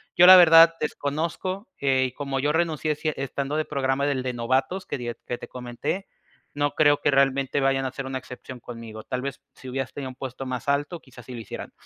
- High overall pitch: No, low, 135 Hz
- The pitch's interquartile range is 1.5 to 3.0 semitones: Yes, average, 2.7 semitones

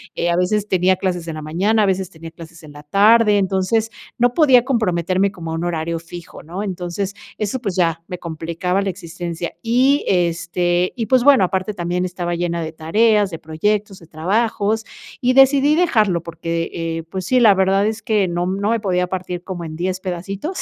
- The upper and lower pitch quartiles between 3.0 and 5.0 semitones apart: Yes, average, 3.7 semitones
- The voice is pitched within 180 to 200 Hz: Yes, medium, 185 Hz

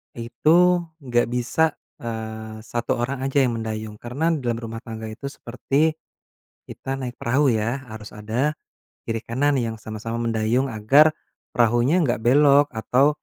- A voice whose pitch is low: Yes, low, 120 Hz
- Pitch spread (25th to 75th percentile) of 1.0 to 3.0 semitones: No, average, 3.7 semitones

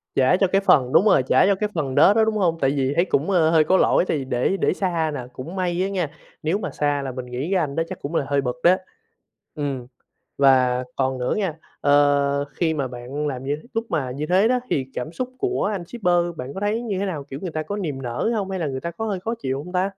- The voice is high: No, medium, 155 Hz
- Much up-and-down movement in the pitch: Yes, wide, 5.8 semitones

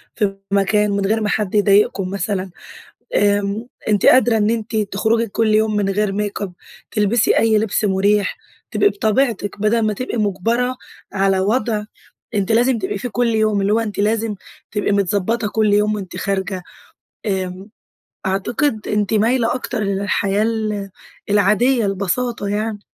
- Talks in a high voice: Yes, high, 210 Hz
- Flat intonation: Yes, narrow, 2.0 semitones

